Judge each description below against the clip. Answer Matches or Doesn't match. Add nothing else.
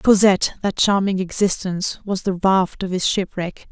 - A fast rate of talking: Doesn't match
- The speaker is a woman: Matches